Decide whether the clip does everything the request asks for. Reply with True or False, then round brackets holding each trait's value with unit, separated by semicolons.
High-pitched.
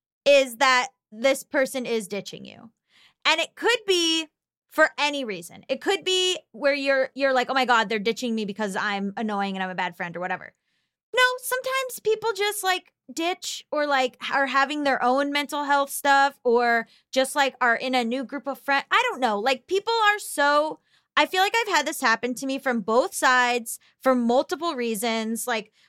True (270 Hz)